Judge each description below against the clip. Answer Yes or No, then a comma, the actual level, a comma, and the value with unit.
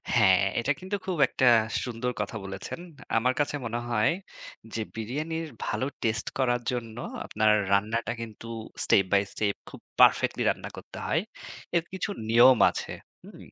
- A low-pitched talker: Yes, low, 115 Hz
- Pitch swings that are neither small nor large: Yes, average, 3.3 semitones